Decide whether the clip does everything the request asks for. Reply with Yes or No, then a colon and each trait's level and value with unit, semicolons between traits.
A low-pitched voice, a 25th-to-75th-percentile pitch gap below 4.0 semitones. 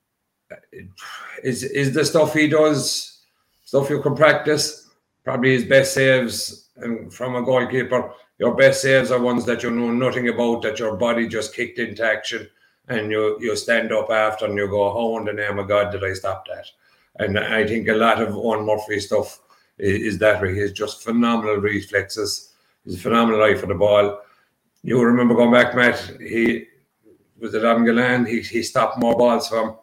Yes: low, 115 Hz; average, 2.8 semitones